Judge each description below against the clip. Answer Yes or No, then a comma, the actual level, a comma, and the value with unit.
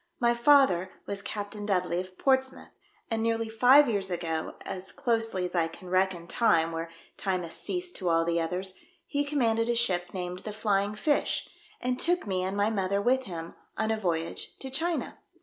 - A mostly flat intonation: No, average, 4.9 semitones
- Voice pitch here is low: No, high, 200 Hz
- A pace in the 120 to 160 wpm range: No, average, 185 wpm